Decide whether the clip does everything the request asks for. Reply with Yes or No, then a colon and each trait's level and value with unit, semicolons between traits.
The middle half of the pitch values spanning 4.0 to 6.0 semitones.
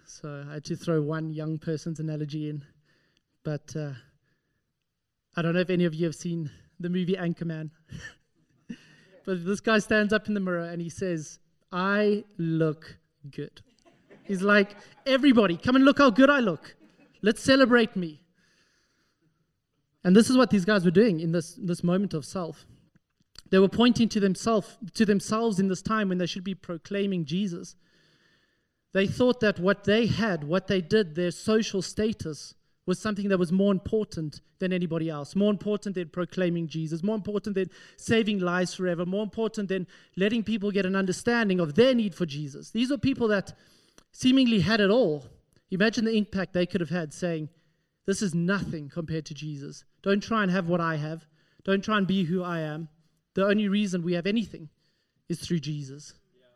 Yes: average, 4.3 semitones